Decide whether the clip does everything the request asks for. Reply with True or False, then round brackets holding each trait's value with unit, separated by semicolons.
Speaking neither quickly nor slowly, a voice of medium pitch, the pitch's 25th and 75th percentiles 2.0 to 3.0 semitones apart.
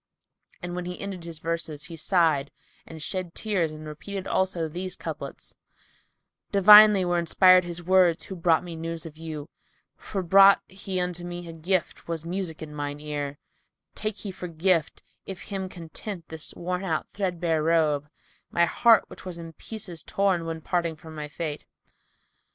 True (175 wpm; 170 Hz; 2.7 semitones)